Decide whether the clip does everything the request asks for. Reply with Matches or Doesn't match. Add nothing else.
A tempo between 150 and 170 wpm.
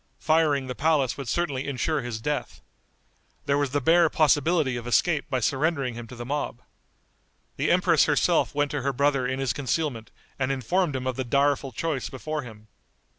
Doesn't match